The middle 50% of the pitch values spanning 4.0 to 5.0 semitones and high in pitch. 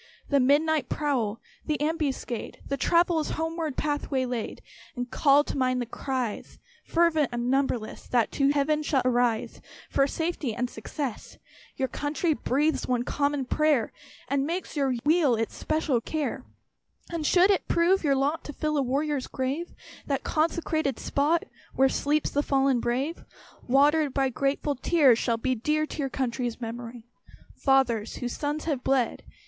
No: average, 3.4 semitones; very high, 275 Hz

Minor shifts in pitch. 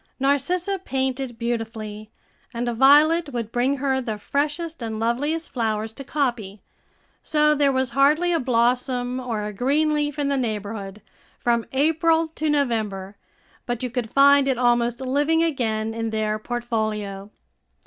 No: average, 4.2 semitones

